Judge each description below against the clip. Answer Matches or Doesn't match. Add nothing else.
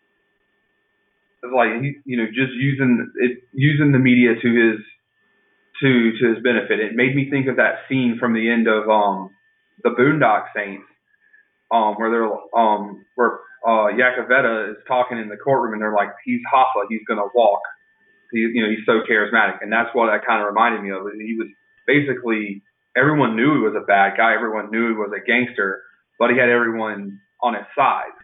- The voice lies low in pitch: Matches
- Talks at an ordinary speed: Matches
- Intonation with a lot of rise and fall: Doesn't match